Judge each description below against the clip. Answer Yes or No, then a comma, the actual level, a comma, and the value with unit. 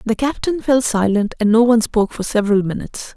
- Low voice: No, high, 225 Hz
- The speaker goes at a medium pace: No, fast, 210 wpm